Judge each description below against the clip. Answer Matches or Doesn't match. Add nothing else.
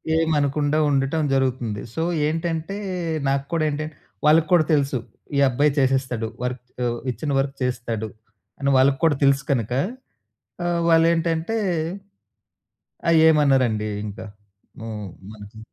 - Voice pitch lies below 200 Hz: Matches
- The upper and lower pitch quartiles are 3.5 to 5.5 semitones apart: Matches